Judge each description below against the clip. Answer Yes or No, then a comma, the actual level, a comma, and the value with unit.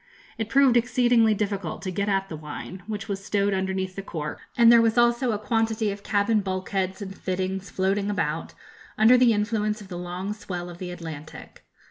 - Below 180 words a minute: No, average, 190 wpm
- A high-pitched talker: Yes, high, 200 Hz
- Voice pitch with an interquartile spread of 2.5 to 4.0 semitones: Yes, average, 2.9 semitones